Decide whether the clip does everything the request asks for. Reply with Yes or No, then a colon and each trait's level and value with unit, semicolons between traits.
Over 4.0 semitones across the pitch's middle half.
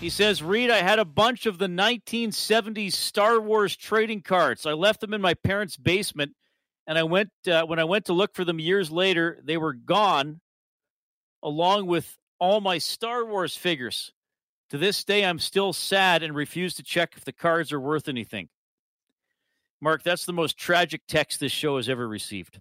Yes: average, 4.8 semitones